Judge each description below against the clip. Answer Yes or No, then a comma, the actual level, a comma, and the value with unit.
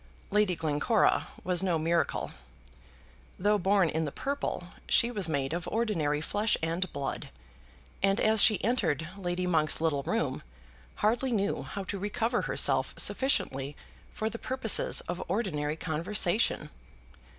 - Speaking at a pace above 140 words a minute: No, slow, 135 wpm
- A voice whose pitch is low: No, medium, 185 Hz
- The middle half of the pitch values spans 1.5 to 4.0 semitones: No, average, 5.0 semitones